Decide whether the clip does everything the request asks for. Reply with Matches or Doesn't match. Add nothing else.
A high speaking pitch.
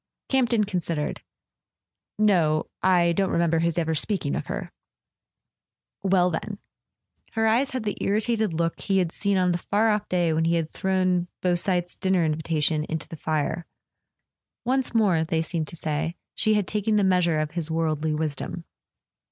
Doesn't match